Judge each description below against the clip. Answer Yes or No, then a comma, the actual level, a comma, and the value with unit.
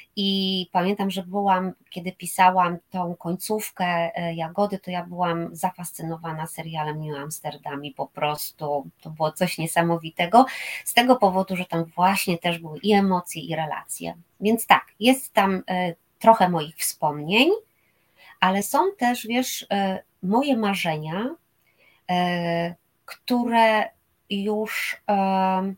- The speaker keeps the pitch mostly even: No, average, 3.2 semitones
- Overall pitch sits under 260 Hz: Yes, medium, 185 Hz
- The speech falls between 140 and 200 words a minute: No, average, 125 wpm